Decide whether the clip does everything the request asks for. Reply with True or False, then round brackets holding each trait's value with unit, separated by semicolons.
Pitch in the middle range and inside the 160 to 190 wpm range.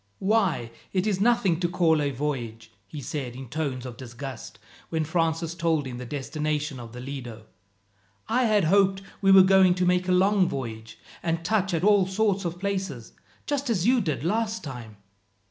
True (165 Hz; 180 wpm)